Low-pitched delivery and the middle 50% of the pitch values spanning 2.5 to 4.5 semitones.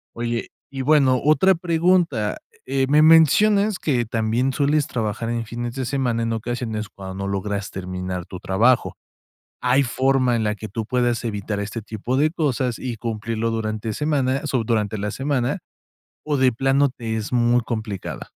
Yes: low, 120 Hz; average, 3.8 semitones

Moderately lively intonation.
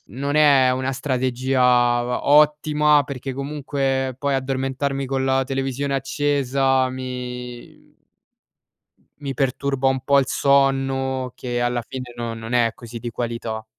No: narrow, 1.8 semitones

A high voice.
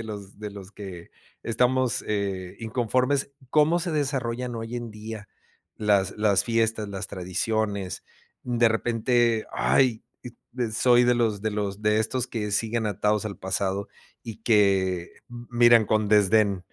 No: low, 110 Hz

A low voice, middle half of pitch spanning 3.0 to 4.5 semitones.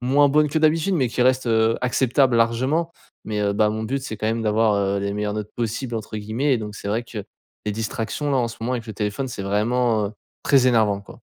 Yes: low, 115 Hz; average, 3.4 semitones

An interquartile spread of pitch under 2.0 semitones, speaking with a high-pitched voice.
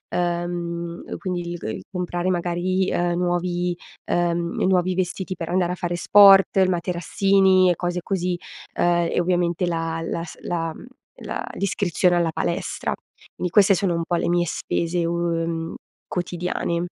No: narrow, 1.1 semitones; medium, 175 Hz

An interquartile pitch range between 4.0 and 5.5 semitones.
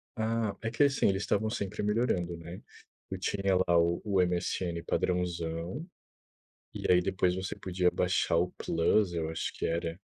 No: average, 2.8 semitones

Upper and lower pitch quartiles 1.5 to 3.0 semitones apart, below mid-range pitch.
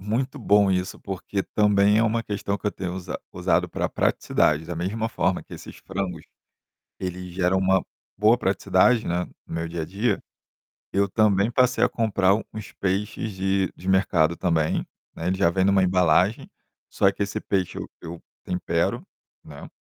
Yes: narrow, 2.5 semitones; very low, 95 Hz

